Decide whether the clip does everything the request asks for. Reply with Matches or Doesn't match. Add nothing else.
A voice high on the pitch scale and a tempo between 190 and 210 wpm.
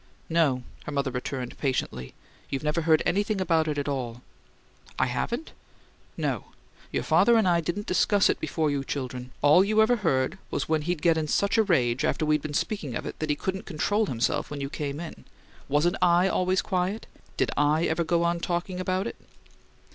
Doesn't match